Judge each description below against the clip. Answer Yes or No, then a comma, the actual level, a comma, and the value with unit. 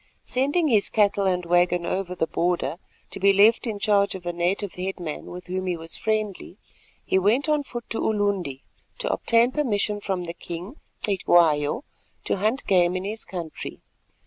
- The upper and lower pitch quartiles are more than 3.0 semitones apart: Yes, average, 3.6 semitones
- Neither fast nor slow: Yes, average, 175 wpm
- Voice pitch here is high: Yes, high, 195 Hz